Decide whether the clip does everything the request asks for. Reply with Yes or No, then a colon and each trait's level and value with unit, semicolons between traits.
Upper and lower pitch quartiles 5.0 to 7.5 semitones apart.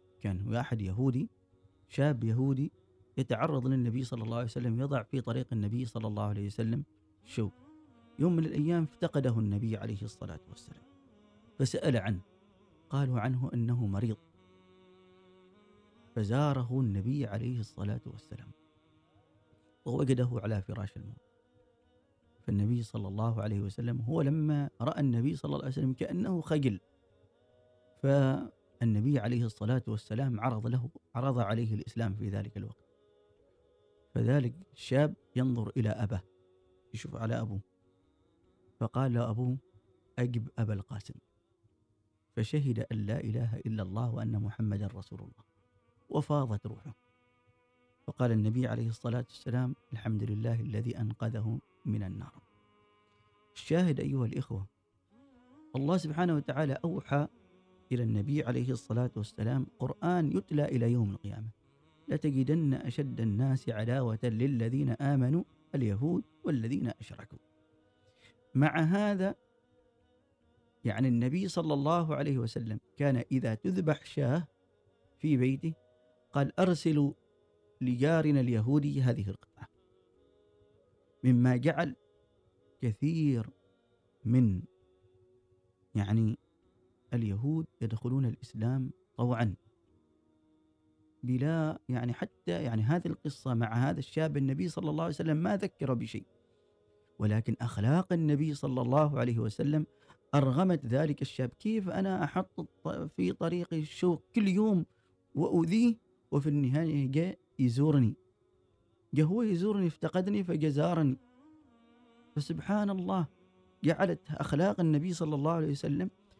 Yes: wide, 5.4 semitones